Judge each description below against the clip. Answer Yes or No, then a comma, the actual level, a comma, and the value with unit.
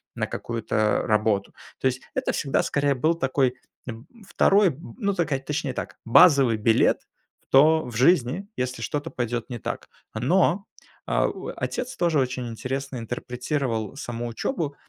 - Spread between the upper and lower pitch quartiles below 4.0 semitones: No, average, 4.3 semitones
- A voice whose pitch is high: No, low, 130 Hz